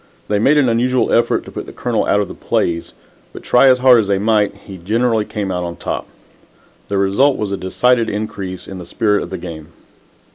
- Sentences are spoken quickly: Yes, fast, 220 wpm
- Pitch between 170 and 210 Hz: No, low, 105 Hz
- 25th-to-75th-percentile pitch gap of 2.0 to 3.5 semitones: No, average, 3.9 semitones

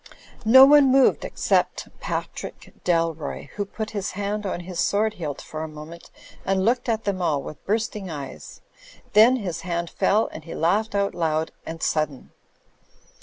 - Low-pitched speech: No, high, 190 Hz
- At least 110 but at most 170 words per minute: Yes, average, 165 wpm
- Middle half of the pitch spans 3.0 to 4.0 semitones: No, average, 4.9 semitones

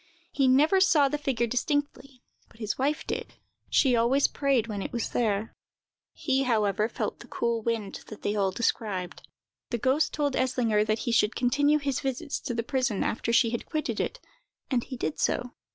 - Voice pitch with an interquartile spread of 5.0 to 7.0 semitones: No, average, 3.8 semitones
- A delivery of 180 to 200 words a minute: Yes, average, 185 wpm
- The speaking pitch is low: No, high, 245 Hz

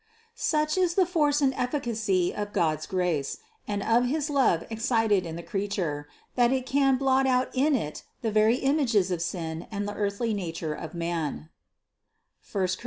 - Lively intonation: Yes, wide, 7.0 semitones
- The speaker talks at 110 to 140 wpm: No, average, 175 wpm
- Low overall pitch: No, high, 215 Hz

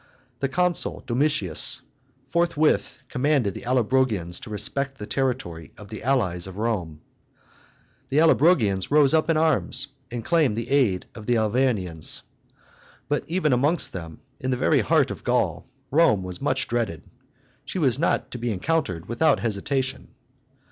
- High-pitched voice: No, low, 125 Hz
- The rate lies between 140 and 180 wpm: Yes, average, 150 wpm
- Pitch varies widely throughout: Yes, wide, 6.2 semitones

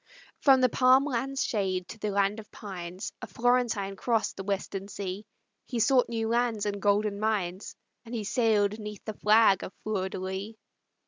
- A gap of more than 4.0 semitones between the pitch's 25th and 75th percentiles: No, average, 2.9 semitones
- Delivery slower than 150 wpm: No, average, 185 wpm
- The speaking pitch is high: Yes, high, 210 Hz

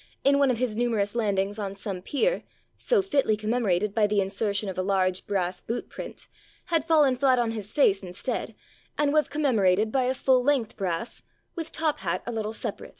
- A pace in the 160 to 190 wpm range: No, fast, 205 wpm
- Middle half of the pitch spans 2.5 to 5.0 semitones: No, wide, 5.5 semitones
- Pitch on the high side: Yes, high, 220 Hz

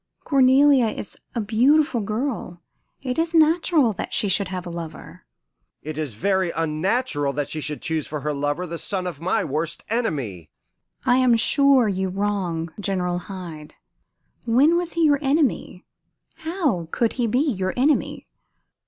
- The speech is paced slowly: No, average, 155 wpm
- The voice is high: Yes, high, 200 Hz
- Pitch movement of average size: No, wide, 7.9 semitones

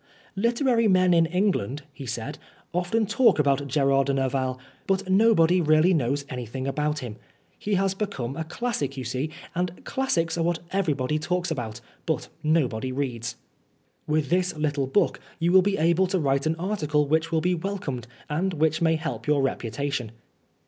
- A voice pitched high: No, medium, 155 Hz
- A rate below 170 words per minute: No, average, 175 wpm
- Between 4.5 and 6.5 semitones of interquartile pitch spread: Yes, average, 4.9 semitones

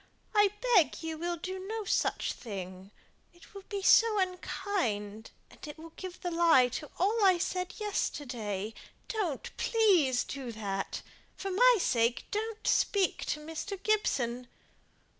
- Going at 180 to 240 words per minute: No, average, 140 wpm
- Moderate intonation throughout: No, wide, 8.5 semitones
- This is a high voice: Yes, very high, 345 Hz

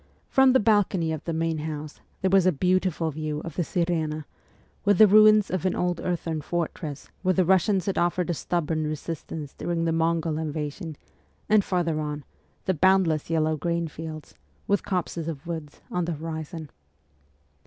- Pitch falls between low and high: Yes, medium, 165 Hz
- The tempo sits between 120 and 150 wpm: No, average, 170 wpm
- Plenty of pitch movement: No, average, 2.9 semitones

